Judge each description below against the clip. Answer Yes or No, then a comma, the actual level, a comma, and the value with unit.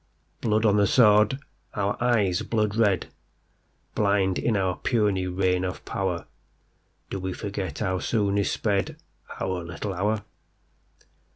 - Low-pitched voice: Yes, low, 100 Hz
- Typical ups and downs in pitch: No, narrow, 2.2 semitones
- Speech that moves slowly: Yes, slow, 115 wpm